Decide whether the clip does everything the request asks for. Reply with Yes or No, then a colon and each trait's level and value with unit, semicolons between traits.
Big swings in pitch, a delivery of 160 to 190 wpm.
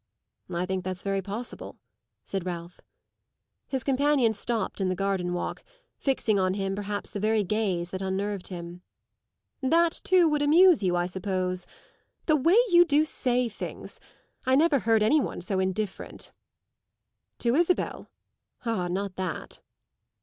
No: wide, 6.1 semitones; average, 145 wpm